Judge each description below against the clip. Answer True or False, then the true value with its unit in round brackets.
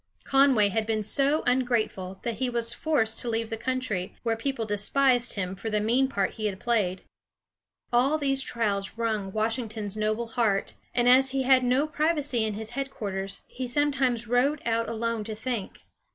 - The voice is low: False (230 Hz)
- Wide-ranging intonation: False (3.3 semitones)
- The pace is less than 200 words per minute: True (175 wpm)